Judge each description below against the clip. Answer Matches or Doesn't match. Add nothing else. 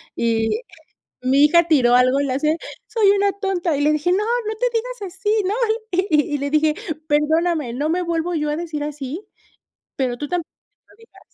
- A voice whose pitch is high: Matches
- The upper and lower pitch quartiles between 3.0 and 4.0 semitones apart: Doesn't match